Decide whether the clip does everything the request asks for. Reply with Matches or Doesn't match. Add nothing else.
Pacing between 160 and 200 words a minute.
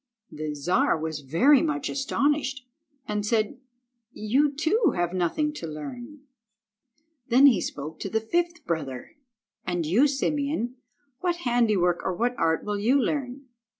Doesn't match